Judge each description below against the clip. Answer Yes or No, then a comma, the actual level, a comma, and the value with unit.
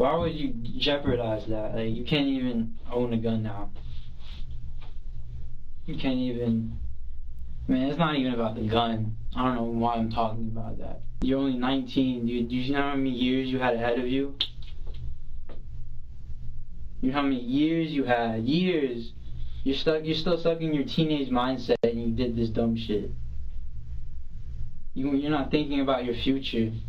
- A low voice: Yes, low, 115 Hz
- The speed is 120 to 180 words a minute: Yes, average, 170 wpm